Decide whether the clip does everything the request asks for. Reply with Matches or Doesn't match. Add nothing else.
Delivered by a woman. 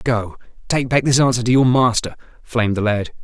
Doesn't match